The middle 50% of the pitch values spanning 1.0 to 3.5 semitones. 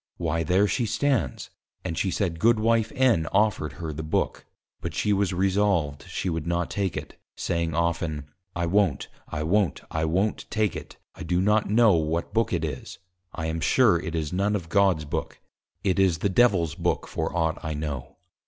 No: average, 4.3 semitones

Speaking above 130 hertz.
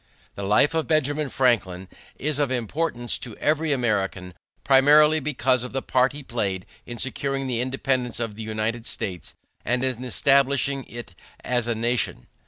No: low, 125 Hz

